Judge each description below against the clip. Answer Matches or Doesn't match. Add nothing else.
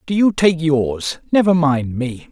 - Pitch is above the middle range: Doesn't match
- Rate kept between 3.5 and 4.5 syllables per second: Matches